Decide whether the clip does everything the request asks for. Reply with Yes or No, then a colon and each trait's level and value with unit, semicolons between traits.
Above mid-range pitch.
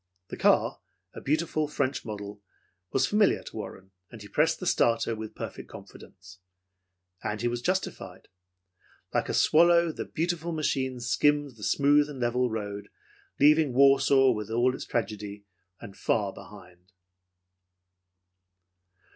No: low, 125 Hz